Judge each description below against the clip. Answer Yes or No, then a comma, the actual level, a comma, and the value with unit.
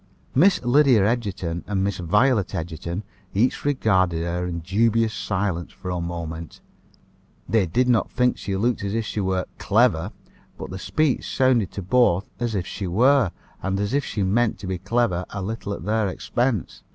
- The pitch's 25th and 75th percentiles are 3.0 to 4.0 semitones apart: No, average, 4.7 semitones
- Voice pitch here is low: Yes, low, 100 Hz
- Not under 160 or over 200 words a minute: Yes, average, 175 wpm